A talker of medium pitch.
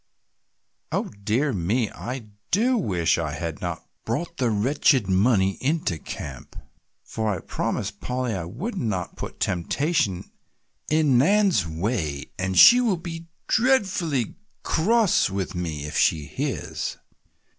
No: low, 115 Hz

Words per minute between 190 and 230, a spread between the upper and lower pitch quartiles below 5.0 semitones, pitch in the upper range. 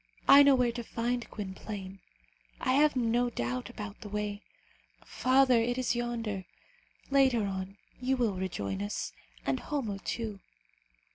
No: average, 140 wpm; average, 4.2 semitones; high, 230 Hz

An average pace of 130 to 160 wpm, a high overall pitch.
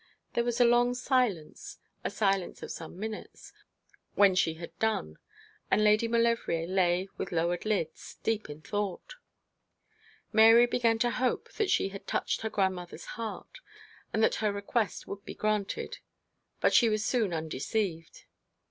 Yes: average, 150 wpm; high, 210 Hz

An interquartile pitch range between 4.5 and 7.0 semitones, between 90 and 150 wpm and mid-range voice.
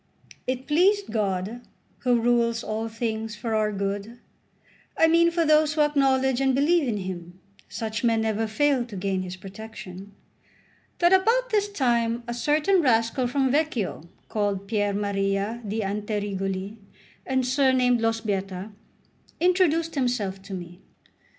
No: average, 5.2 semitones; slow, 135 wpm; high, 230 Hz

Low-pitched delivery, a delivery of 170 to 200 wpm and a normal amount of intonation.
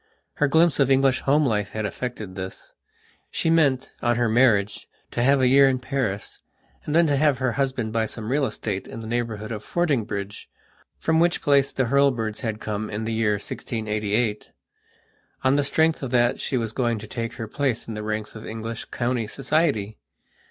Yes: low, 120 Hz; average, 190 wpm; average, 4.0 semitones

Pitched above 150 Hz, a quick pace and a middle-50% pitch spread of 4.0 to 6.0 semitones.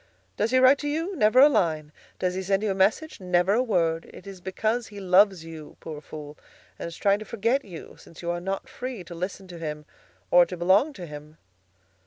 Yes: high, 190 Hz; fast, 225 wpm; average, 4.7 semitones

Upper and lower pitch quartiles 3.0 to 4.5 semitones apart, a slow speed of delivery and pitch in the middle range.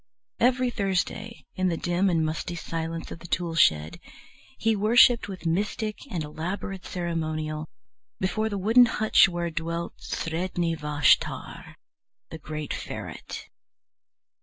Yes: average, 3.9 semitones; slow, 125 wpm; medium, 175 Hz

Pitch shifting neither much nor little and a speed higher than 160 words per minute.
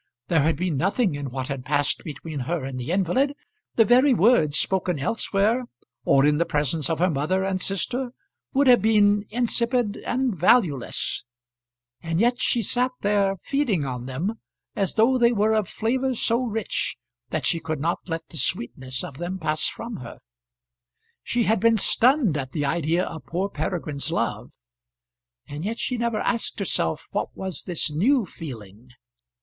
No: wide, 7.3 semitones; average, 170 wpm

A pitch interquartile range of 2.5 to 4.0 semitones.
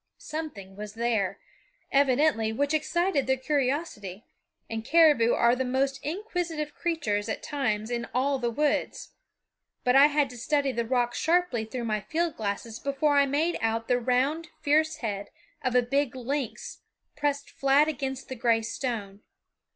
No: average, 4.4 semitones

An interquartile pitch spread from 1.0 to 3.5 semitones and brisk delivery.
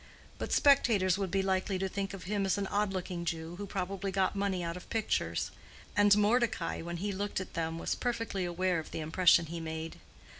Yes: average, 2.8 semitones; fast, 210 wpm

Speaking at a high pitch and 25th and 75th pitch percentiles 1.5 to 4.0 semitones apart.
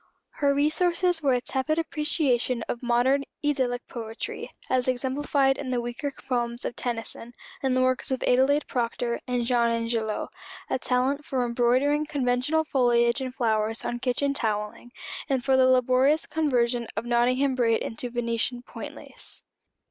Yes: very high, 250 Hz; narrow, 2.5 semitones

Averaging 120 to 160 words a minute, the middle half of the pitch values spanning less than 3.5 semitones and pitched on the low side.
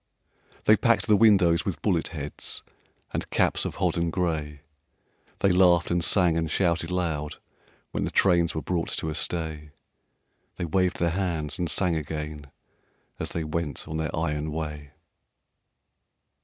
Yes: average, 150 wpm; narrow, 2.6 semitones; very low, 85 Hz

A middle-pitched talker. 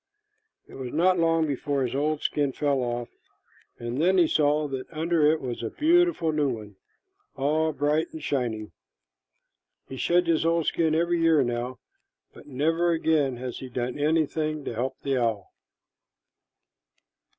Yes: medium, 150 Hz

